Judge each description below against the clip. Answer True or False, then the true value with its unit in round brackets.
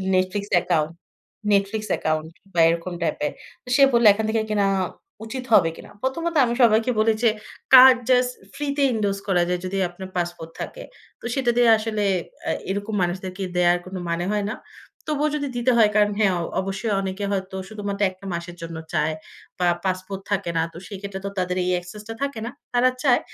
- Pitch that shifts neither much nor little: True (3.7 semitones)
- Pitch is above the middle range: True (200 Hz)